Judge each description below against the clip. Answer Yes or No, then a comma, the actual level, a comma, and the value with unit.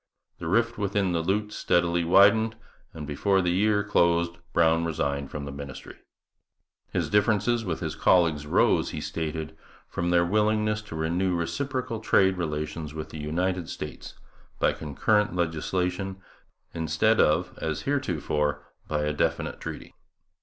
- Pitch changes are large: No, average, 4.6 semitones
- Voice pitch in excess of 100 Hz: No, very low, 85 Hz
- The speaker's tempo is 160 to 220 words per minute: No, average, 140 wpm